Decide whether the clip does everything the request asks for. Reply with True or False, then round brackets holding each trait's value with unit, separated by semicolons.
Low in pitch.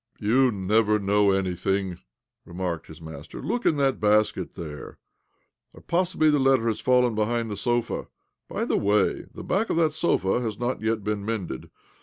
True (105 Hz)